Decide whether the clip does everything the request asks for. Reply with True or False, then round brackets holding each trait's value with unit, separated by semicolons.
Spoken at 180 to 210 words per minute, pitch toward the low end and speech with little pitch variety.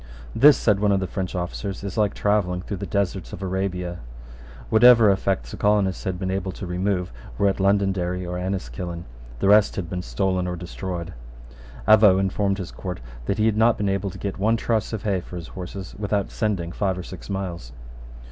True (200 wpm; 95 Hz; 2.2 semitones)